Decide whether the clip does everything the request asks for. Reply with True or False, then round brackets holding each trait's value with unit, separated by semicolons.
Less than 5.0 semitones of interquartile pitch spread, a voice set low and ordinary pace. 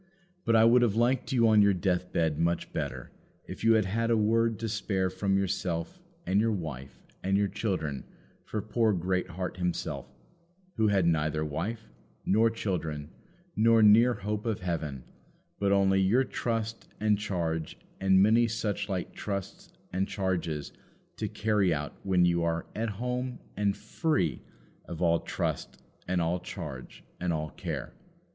True (4.4 semitones; 95 Hz; 155 wpm)